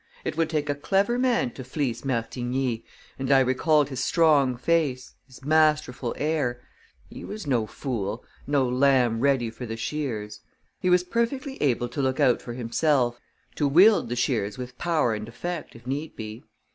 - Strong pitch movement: No, average, 4.2 semitones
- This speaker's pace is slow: No, average, 170 wpm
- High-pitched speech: No, low, 130 Hz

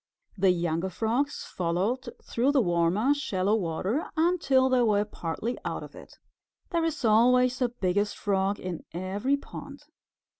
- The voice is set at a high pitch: Yes, high, 220 Hz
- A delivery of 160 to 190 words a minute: No, average, 145 wpm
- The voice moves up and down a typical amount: No, wide, 6.0 semitones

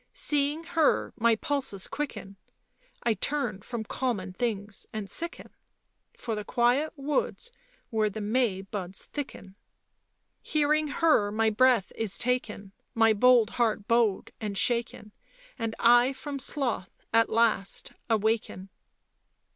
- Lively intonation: No, average, 4.0 semitones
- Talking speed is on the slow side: Yes, slow, 130 wpm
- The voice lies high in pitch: Yes, high, 230 Hz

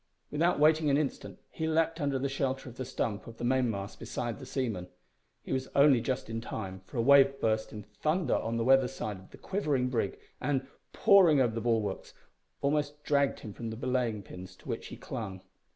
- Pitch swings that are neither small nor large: Yes, average, 4.0 semitones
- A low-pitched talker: Yes, low, 130 Hz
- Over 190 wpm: Yes, fast, 205 wpm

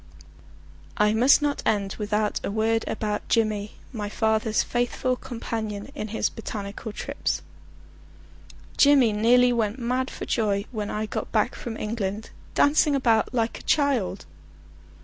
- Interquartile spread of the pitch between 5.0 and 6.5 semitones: No, average, 2.7 semitones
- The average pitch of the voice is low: No, high, 220 Hz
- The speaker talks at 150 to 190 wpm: No, slow, 135 wpm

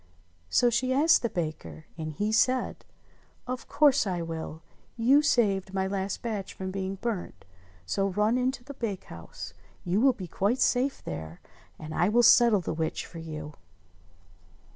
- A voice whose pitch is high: Yes, high, 195 Hz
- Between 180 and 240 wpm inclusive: No, average, 165 wpm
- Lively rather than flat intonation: Yes, wide, 6.4 semitones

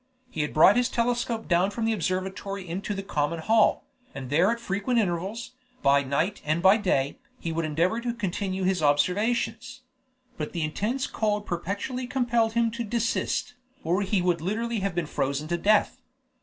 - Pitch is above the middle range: Yes, high, 195 Hz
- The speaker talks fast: No, average, 175 wpm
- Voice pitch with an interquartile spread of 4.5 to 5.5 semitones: Yes, average, 5.2 semitones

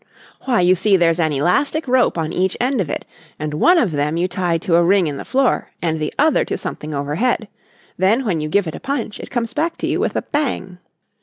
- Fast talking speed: Yes, fast, 240 wpm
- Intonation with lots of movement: Yes, wide, 7.3 semitones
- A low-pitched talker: No, medium, 185 Hz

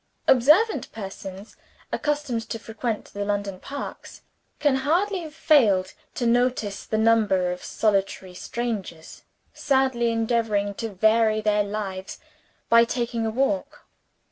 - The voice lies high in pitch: Yes, high, 225 Hz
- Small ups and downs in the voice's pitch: No, average, 4.0 semitones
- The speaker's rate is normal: No, slow, 120 wpm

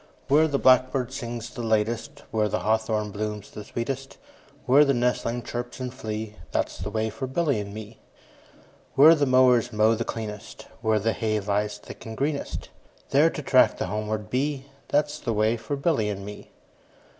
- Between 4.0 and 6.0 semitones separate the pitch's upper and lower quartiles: No, average, 3.4 semitones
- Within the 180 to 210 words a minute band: Yes, average, 190 wpm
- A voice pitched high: No, low, 115 Hz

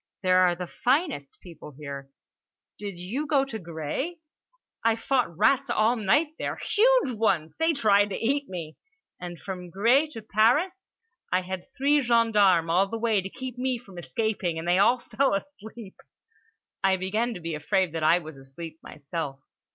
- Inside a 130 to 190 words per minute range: Yes, average, 170 wpm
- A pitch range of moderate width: No, wide, 6.3 semitones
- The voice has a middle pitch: No, high, 200 Hz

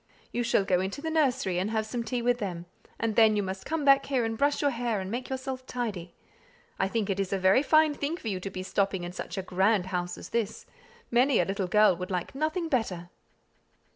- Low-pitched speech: No, high, 220 Hz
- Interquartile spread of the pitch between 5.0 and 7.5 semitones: Yes, average, 5.3 semitones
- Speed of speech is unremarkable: No, fast, 235 wpm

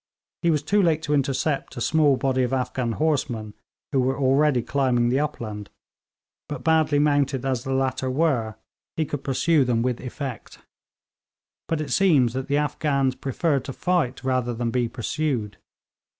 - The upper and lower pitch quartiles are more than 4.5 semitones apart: No, average, 3.1 semitones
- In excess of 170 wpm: No, average, 165 wpm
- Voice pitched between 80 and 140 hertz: Yes, low, 135 Hz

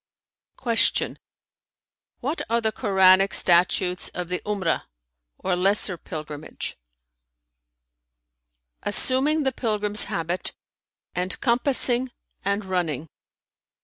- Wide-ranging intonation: No, average, 4.7 semitones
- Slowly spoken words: Yes, slow, 85 wpm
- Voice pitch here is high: Yes, high, 195 Hz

